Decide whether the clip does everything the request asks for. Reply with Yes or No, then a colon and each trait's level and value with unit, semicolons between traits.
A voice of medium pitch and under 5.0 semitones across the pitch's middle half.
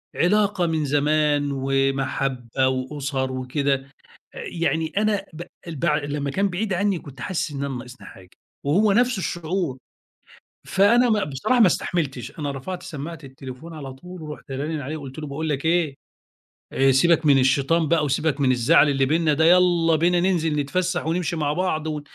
Yes: medium, 150 Hz; average, 4.2 semitones